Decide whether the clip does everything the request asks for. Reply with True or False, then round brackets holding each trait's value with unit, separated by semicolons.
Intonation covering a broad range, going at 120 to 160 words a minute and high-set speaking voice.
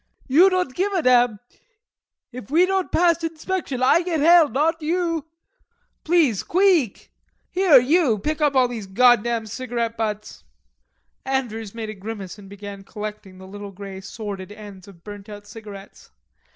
True (7.7 semitones; 150 wpm; 235 Hz)